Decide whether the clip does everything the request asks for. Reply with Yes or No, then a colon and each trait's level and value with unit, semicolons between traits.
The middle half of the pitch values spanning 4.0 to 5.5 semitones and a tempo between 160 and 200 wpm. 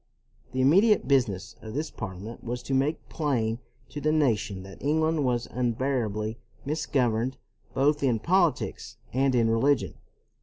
No: average, 4.6 semitones; average, 140 wpm